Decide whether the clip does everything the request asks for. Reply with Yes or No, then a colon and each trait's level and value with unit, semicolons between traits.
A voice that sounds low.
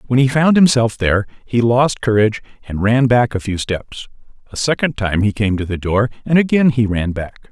Yes: low, 115 Hz